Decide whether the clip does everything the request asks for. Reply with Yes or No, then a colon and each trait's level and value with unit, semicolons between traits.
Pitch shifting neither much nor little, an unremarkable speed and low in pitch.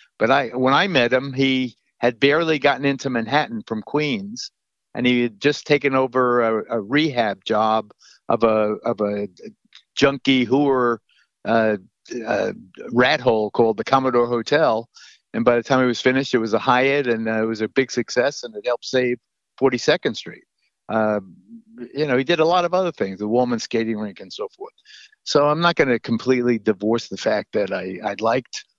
Yes: average, 4.1 semitones; average, 190 wpm; low, 125 Hz